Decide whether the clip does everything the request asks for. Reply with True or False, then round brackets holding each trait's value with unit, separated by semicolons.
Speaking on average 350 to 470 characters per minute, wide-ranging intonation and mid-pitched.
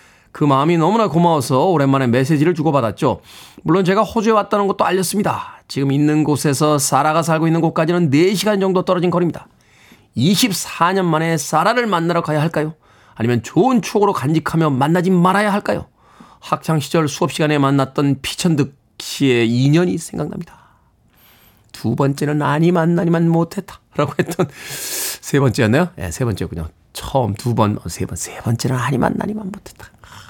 False (360 characters per minute; 5.0 semitones; 155 Hz)